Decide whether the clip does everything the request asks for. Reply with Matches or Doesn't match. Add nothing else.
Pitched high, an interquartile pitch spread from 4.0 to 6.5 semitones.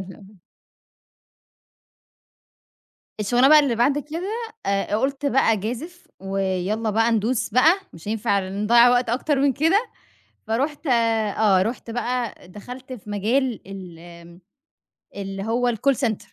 Matches